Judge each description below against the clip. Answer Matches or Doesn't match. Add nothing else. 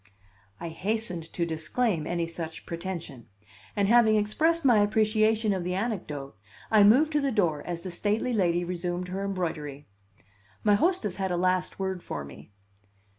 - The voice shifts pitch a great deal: Doesn't match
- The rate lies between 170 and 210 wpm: Doesn't match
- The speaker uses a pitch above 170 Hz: Matches